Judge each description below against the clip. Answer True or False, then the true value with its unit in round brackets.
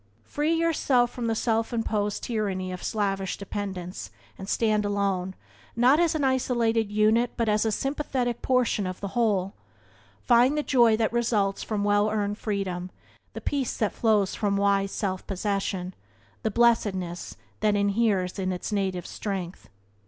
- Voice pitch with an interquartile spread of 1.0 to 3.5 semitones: True (3.2 semitones)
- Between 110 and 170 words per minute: True (150 wpm)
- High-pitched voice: True (210 Hz)